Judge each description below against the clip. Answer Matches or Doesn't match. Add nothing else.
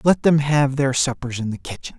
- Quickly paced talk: Matches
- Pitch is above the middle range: Doesn't match